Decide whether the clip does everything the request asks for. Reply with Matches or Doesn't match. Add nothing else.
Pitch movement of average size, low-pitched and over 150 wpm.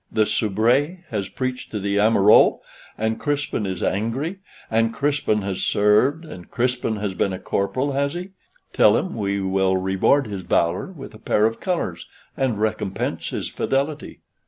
Doesn't match